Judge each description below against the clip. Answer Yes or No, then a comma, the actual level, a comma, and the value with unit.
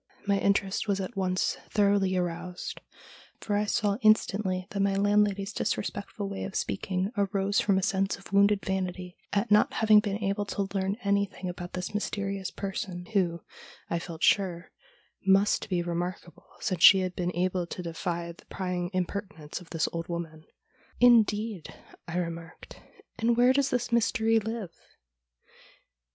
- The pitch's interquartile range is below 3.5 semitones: Yes, narrow, 2.4 semitones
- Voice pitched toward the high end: Yes, high, 195 Hz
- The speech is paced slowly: No, average, 165 wpm